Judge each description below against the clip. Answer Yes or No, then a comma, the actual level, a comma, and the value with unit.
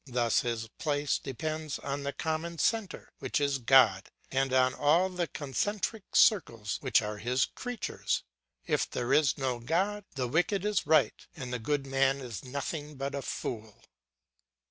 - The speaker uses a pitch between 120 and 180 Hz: Yes, medium, 140 Hz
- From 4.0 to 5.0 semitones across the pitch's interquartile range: Yes, average, 4.3 semitones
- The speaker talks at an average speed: Yes, average, 160 wpm